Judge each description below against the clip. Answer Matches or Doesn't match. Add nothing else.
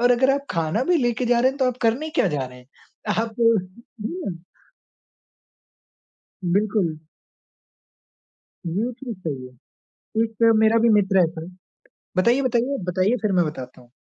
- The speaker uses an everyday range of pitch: Doesn't match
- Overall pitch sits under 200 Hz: Doesn't match